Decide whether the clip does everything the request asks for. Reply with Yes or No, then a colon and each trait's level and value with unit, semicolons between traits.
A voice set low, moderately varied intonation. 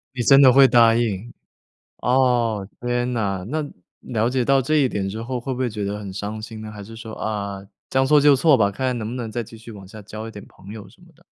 Yes: low, 115 Hz; average, 3.4 semitones